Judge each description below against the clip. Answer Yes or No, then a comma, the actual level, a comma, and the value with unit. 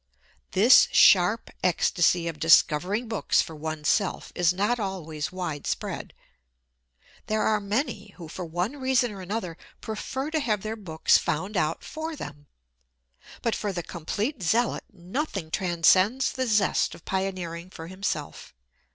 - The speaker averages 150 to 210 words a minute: No, average, 140 wpm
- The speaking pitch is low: No, high, 190 Hz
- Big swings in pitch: No, average, 4.7 semitones